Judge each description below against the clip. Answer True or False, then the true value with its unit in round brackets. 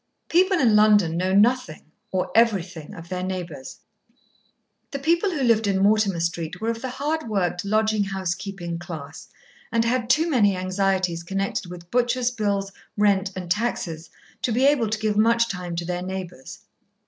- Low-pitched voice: False (200 Hz)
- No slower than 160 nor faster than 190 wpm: True (170 wpm)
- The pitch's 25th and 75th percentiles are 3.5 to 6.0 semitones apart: True (4.5 semitones)